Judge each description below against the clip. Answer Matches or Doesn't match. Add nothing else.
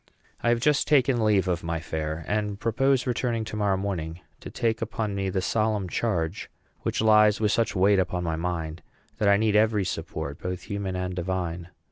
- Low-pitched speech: Matches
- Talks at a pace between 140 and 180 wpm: Doesn't match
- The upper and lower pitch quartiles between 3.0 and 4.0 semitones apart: Matches